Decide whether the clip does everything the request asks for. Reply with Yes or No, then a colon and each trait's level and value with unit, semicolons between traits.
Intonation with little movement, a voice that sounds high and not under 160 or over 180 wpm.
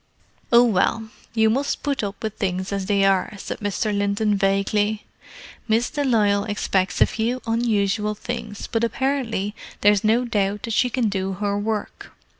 Yes: narrow, 2.3 semitones; high, 210 Hz; average, 170 wpm